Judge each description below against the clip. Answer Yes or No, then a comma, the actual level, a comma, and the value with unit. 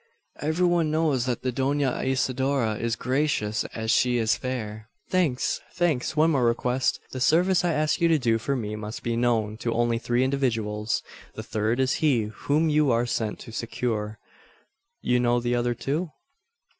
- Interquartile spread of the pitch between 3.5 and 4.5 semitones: Yes, average, 3.9 semitones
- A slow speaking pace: No, average, 175 wpm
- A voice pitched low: Yes, low, 125 Hz